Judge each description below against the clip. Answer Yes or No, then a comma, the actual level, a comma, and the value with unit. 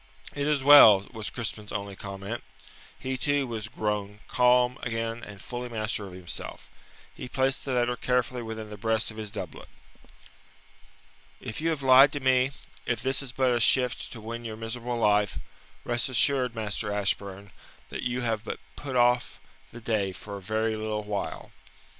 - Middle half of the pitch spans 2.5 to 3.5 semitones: Yes, average, 3.0 semitones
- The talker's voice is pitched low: Yes, low, 115 Hz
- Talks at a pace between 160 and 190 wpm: Yes, average, 170 wpm